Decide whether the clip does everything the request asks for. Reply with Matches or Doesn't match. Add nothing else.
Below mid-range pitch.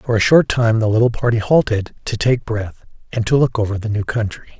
Matches